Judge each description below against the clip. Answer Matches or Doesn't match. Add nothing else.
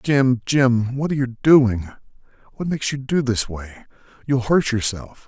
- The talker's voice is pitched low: Matches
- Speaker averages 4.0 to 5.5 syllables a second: Matches